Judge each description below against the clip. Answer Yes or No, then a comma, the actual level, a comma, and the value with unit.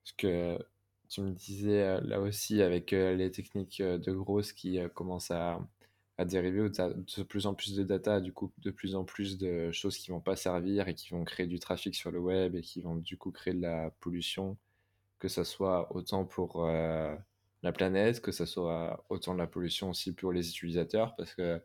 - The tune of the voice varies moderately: No, narrow, 2.2 semitones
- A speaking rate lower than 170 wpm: No, average, 215 wpm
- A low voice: Yes, very low, 95 Hz